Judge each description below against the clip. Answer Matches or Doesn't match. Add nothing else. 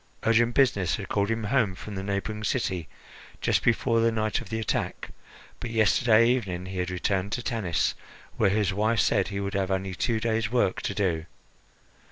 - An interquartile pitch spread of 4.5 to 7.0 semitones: Doesn't match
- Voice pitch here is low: Matches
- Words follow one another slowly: Doesn't match